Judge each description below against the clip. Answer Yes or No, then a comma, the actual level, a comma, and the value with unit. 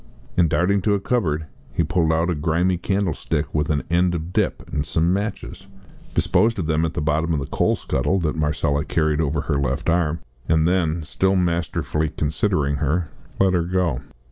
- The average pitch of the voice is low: Yes, very low, 80 Hz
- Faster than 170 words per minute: Yes, average, 190 wpm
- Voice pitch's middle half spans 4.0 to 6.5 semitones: No, average, 2.9 semitones